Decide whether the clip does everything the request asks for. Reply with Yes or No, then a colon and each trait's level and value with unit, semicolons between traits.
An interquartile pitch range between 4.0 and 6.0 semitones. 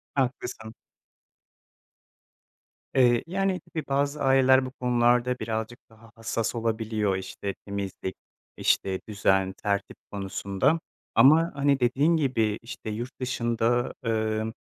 No: average, 3.4 semitones